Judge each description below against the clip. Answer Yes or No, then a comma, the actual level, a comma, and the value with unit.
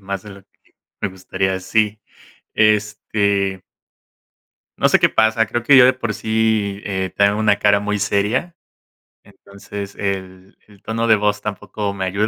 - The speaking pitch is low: Yes, low, 105 Hz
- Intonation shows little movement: Yes, narrow, 1.7 semitones